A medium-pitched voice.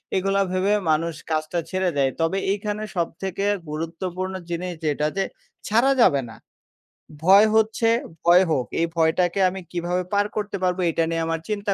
Yes: medium, 180 Hz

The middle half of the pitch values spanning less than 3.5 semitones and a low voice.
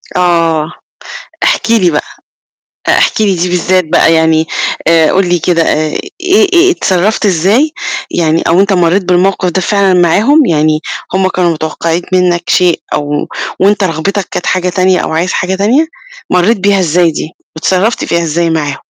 No: average, 2.9 semitones; medium, 180 Hz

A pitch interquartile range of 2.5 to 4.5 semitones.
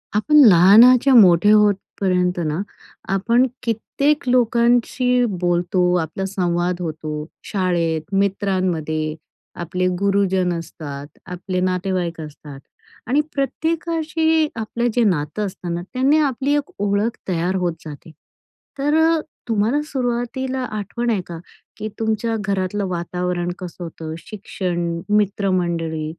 No: average, 5.3 semitones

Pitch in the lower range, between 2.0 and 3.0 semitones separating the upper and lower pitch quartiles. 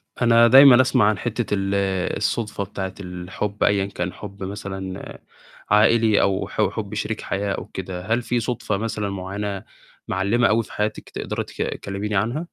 Yes: low, 105 Hz; average, 2.7 semitones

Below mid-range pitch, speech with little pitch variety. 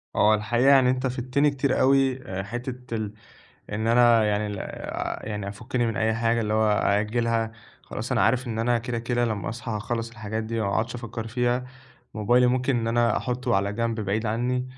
Yes: low, 115 Hz; narrow, 2.2 semitones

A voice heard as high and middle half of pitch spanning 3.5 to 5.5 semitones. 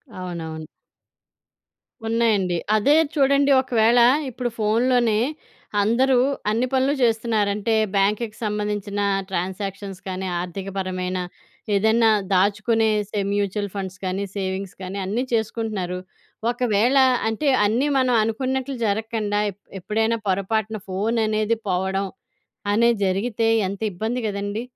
No: high, 210 Hz; average, 3.0 semitones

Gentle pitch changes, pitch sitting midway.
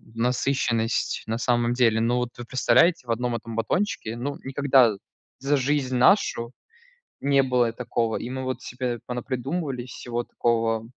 No: narrow, 2.1 semitones; low, 125 Hz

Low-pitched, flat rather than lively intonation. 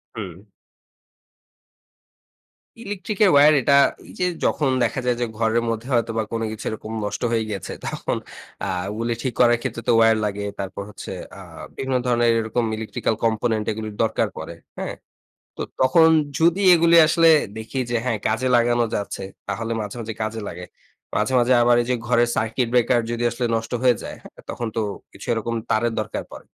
Yes: low, 115 Hz; narrow, 2.1 semitones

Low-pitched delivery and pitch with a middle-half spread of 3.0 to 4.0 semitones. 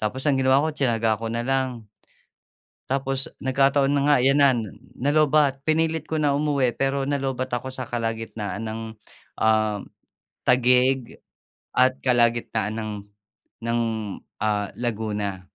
Yes: low, 130 Hz; average, 3.3 semitones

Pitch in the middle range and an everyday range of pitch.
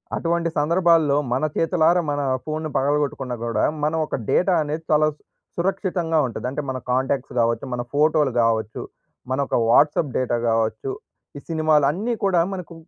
Yes: medium, 150 Hz; average, 4.3 semitones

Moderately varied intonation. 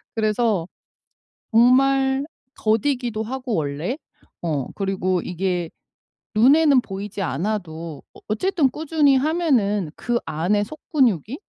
No: wide, 6.3 semitones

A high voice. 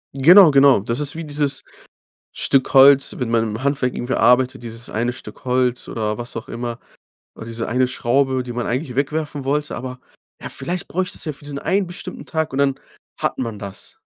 No: low, 130 Hz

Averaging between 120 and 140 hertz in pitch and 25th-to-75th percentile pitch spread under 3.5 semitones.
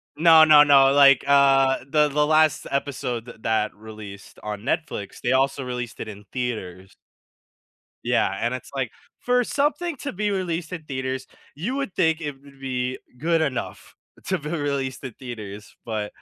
No: low, 135 Hz; average, 4.5 semitones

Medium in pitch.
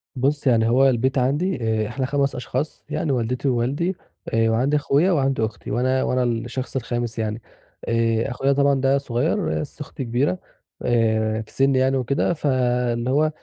No: low, 130 Hz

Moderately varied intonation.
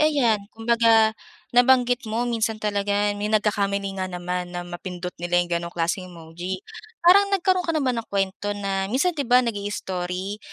Yes: average, 4.6 semitones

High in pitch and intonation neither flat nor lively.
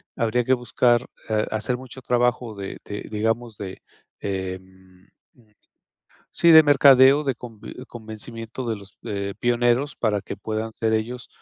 No: low, 115 Hz; average, 3.0 semitones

